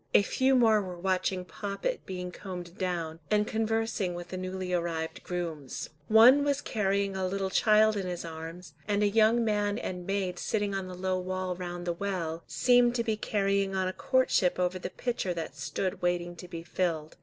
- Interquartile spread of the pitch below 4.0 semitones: Yes, average, 2.9 semitones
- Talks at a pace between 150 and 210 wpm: Yes, average, 190 wpm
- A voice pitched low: No, medium, 185 Hz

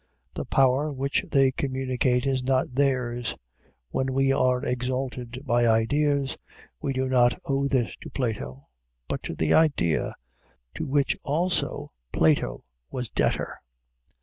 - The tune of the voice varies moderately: No, narrow, 1.9 semitones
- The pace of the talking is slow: Yes, slow, 130 wpm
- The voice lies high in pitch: No, low, 130 Hz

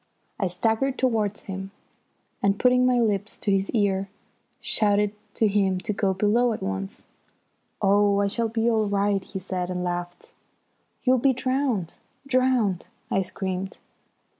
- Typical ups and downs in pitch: Yes, average, 3.4 semitones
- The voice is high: Yes, high, 205 Hz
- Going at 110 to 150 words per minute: Yes, average, 145 wpm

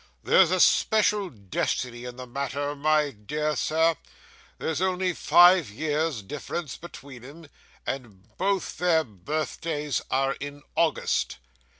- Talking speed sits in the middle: No, slow, 120 wpm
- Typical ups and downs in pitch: Yes, average, 4.5 semitones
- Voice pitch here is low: No, medium, 150 Hz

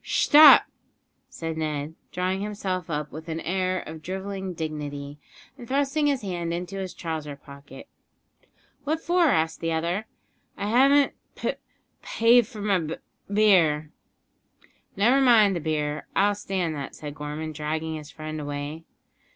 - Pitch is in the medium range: Yes, medium, 170 Hz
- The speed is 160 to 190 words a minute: No, average, 145 wpm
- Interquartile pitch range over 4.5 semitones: Yes, average, 5.0 semitones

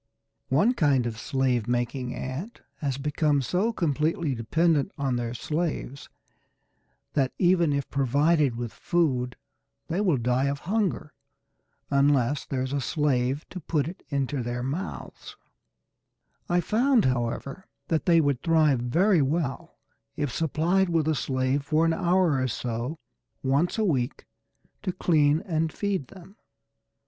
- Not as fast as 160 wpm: Yes, average, 140 wpm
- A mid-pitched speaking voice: Yes, medium, 145 Hz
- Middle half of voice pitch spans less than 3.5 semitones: No, average, 4.5 semitones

